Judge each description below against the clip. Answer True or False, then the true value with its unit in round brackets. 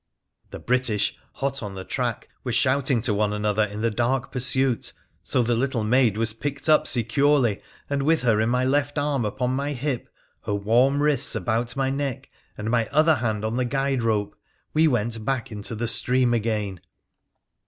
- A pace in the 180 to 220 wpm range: True (185 wpm)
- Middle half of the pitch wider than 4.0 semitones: False (3.7 semitones)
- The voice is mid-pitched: False (120 Hz)